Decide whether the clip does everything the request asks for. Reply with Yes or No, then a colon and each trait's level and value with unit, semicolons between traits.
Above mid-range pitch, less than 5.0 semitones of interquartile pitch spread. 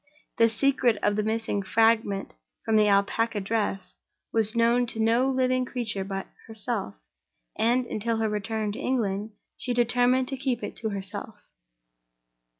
Yes: high, 225 Hz; average, 2.8 semitones